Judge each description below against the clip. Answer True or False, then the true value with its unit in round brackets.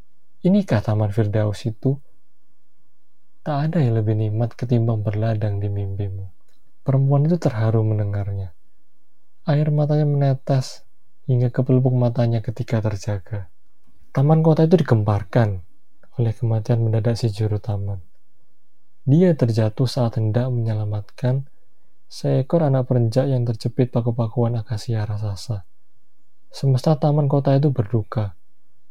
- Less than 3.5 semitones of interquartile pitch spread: False (3.9 semitones)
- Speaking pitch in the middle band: False (120 Hz)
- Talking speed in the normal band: True (110 wpm)